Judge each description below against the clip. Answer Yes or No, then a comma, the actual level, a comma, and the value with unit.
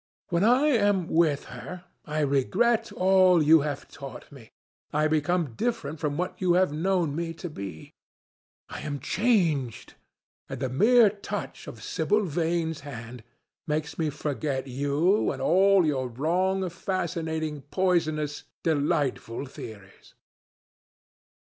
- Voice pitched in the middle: Yes, medium, 160 Hz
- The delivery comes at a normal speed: No, slow, 130 wpm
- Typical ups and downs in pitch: Yes, average, 4.4 semitones